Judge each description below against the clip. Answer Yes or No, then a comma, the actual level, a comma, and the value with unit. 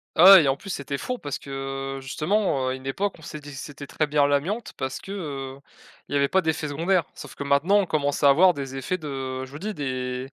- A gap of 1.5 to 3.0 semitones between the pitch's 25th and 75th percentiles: No, average, 3.8 semitones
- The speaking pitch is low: No, medium, 145 Hz